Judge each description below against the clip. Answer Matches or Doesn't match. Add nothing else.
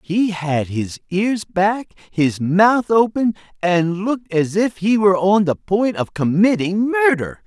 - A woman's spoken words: Doesn't match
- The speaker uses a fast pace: Doesn't match